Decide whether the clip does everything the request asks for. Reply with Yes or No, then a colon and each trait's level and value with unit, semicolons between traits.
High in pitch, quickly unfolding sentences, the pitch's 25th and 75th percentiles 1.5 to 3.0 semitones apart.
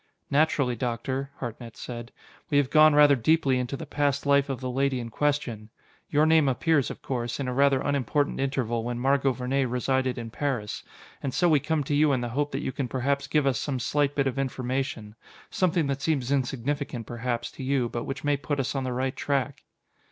No: low, 135 Hz; fast, 210 wpm; narrow, 2.5 semitones